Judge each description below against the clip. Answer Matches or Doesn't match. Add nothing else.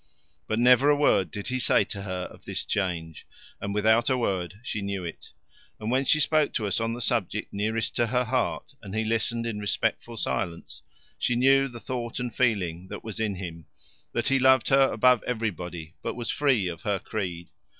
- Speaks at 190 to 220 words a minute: Matches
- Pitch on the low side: Matches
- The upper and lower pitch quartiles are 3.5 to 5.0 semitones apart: Matches